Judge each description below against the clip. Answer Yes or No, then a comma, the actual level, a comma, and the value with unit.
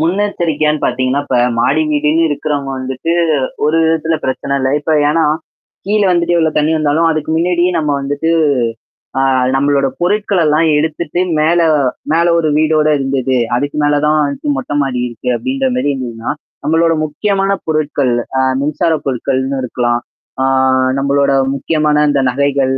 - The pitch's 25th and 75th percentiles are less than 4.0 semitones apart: Yes, average, 3.0 semitones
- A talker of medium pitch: Yes, medium, 150 Hz